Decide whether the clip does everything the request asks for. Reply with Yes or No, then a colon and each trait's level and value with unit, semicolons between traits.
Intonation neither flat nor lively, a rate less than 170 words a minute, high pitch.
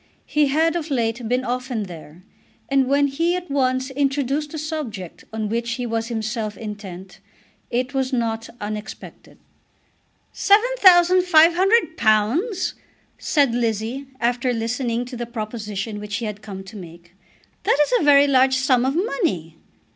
Yes: average, 4.8 semitones; average, 155 wpm; very high, 250 Hz